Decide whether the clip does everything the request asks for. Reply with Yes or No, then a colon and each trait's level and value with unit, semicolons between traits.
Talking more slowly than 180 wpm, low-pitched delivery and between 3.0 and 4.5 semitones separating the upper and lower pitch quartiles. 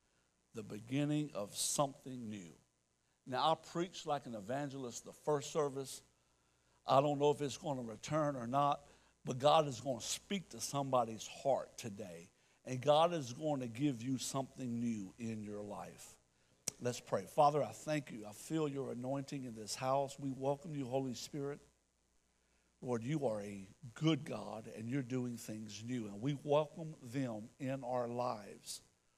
No: average, 170 wpm; low, 130 Hz; average, 4.9 semitones